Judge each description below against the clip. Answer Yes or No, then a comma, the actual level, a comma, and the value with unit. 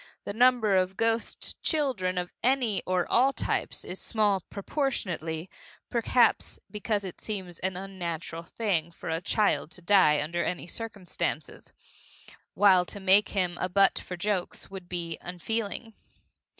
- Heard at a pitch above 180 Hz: Yes, high, 190 Hz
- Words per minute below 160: Yes, average, 145 wpm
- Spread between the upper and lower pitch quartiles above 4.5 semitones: No, average, 3.6 semitones